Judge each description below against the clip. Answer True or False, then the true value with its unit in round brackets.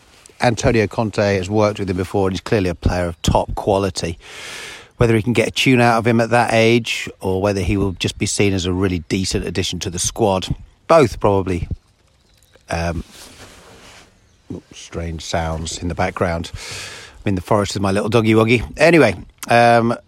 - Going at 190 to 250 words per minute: False (180 wpm)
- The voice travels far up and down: False (3.5 semitones)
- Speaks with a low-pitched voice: True (100 Hz)